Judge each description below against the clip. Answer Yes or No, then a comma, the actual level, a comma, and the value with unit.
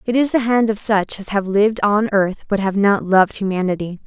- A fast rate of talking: Yes, fast, 235 wpm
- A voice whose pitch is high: Yes, high, 205 Hz